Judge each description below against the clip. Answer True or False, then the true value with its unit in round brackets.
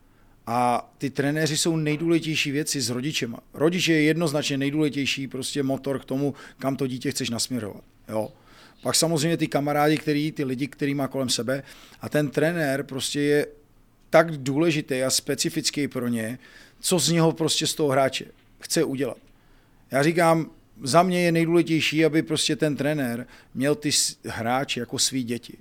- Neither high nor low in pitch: True (145 Hz)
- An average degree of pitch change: True (3.0 semitones)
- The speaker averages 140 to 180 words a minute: True (160 wpm)